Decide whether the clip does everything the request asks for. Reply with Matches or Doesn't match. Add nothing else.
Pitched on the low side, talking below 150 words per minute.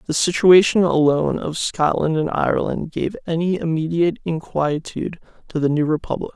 Doesn't match